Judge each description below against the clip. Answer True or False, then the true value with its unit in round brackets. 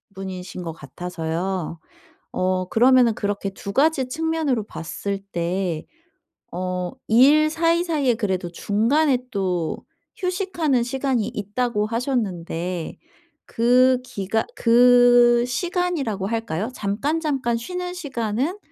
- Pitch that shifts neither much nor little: False (6.4 semitones)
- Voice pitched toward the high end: True (230 Hz)